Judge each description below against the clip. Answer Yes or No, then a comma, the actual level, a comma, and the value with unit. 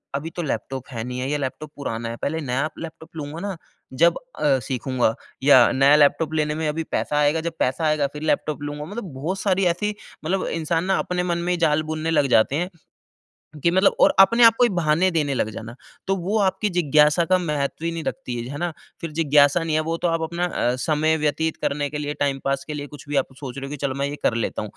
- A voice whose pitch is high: No, medium, 150 Hz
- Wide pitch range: No, average, 3.1 semitones